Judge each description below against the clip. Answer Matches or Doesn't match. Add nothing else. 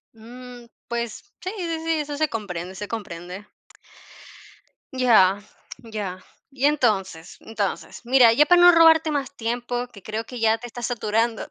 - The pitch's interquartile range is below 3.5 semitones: Doesn't match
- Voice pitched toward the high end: Matches